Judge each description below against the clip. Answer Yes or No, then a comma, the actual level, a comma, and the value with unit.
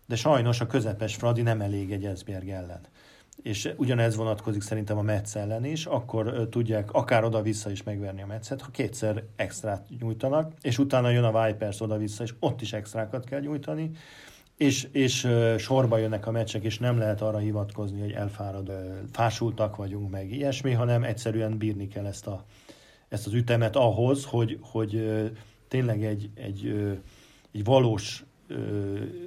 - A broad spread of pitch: No, average, 2.7 semitones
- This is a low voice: Yes, low, 110 Hz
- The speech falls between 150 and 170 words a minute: Yes, fast, 155 wpm